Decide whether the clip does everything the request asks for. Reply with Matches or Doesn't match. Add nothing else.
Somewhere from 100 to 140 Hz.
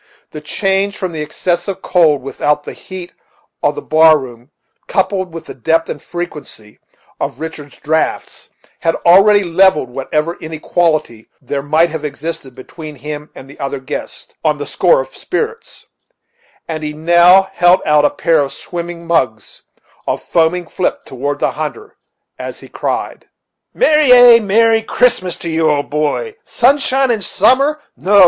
Doesn't match